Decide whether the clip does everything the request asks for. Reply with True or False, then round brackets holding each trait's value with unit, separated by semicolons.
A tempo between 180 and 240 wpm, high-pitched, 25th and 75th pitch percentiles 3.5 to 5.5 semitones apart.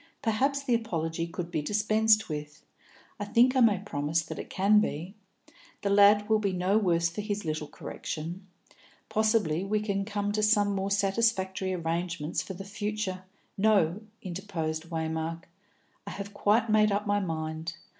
False (165 wpm; 195 Hz; 4.1 semitones)